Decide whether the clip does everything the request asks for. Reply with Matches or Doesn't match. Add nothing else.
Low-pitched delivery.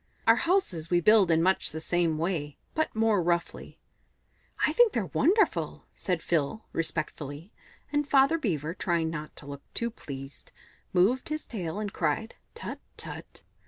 Doesn't match